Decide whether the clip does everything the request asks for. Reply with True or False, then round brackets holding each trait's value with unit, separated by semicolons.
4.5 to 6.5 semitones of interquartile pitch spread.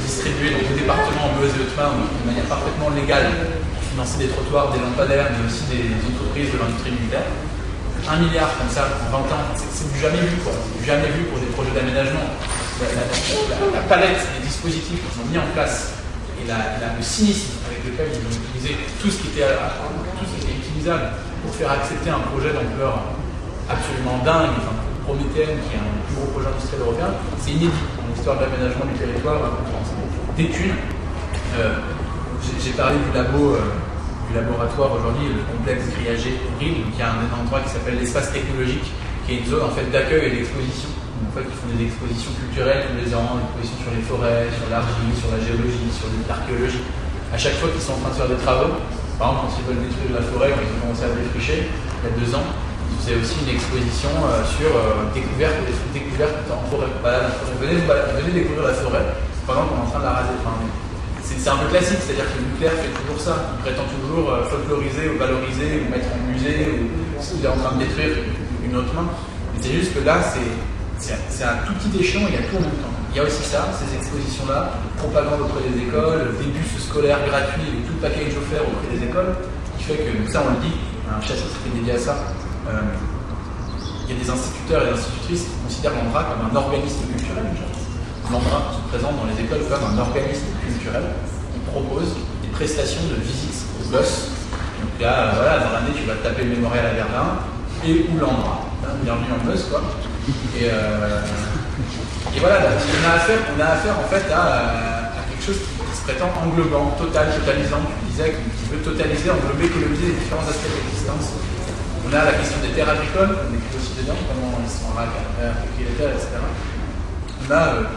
True (5.2 semitones)